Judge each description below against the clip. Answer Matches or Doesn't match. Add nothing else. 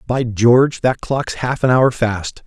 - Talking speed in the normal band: Matches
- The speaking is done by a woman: Doesn't match